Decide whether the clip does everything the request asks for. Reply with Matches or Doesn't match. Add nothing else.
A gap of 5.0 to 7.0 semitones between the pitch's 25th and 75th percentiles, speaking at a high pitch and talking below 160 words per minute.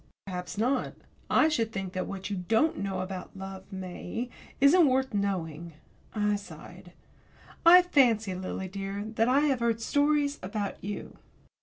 Matches